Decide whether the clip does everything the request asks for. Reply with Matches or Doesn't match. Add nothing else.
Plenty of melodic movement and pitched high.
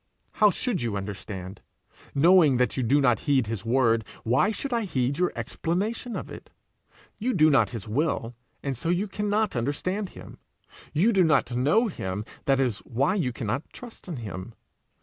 Doesn't match